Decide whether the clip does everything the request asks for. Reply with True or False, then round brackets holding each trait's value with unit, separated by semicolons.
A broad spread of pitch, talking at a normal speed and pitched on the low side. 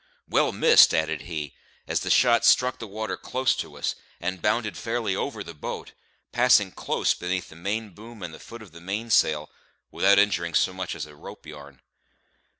True (5.8 semitones; 180 wpm; 95 Hz)